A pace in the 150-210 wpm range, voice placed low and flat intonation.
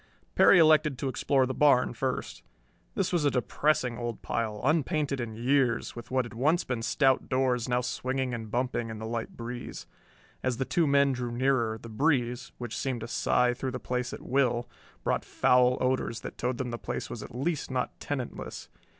Yes: average, 195 wpm; low, 125 Hz; narrow, 2.2 semitones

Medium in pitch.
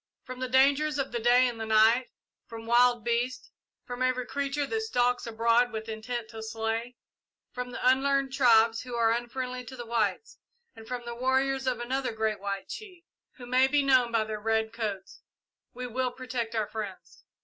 No: high, 245 Hz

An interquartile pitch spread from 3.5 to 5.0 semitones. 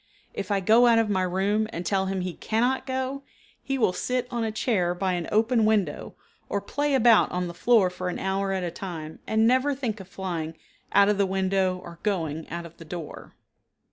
Yes: average, 4.0 semitones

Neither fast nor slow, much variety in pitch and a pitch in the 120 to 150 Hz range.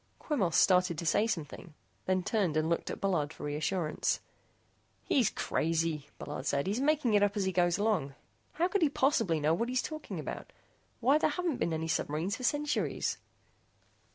No: average, 180 wpm; wide, 7.6 semitones; high, 190 Hz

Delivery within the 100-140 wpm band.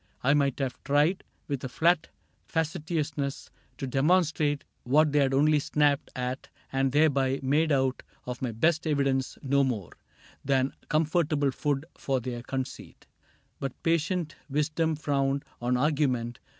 Yes: slow, 135 wpm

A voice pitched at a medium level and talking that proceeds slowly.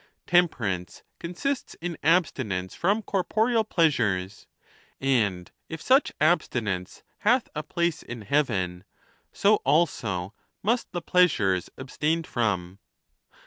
Yes: medium, 150 Hz; slow, 105 wpm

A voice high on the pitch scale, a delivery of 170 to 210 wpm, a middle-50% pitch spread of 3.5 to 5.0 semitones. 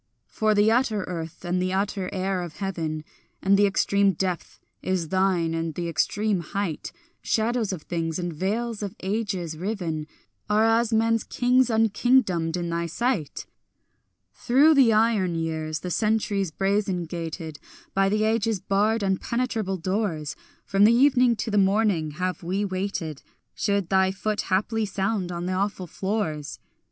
No: high, 195 Hz; average, 150 wpm; average, 3.9 semitones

